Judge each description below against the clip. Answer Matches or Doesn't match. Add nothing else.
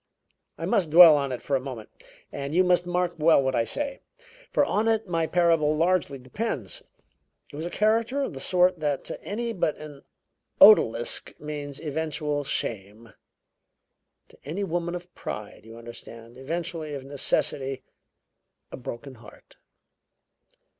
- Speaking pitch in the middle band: Matches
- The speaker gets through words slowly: Doesn't match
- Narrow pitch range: Doesn't match